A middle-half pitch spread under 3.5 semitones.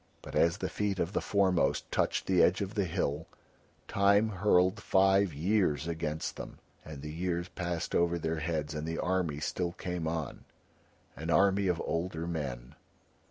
Yes: average, 3.1 semitones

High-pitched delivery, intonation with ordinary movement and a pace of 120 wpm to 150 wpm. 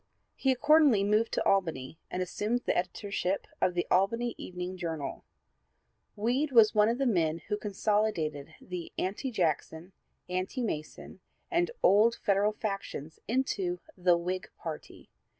Yes: high, 195 Hz; average, 4.2 semitones; slow, 135 wpm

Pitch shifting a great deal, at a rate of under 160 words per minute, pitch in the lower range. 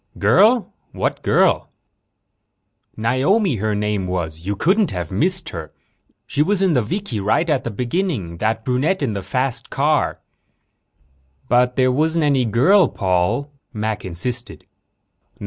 Yes: wide, 7.4 semitones; average, 140 wpm; low, 125 Hz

